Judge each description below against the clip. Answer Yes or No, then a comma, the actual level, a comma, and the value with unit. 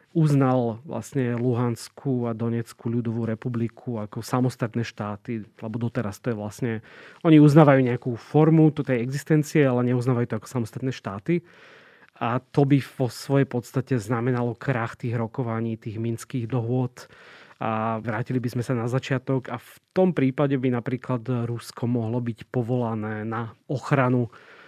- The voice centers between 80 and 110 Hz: No, low, 125 Hz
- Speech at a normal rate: Yes, average, 145 wpm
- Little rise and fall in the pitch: Yes, narrow, 2.2 semitones